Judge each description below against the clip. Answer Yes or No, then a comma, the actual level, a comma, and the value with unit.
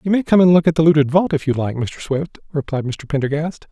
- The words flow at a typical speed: No, fast, 275 wpm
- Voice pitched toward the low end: No, medium, 155 Hz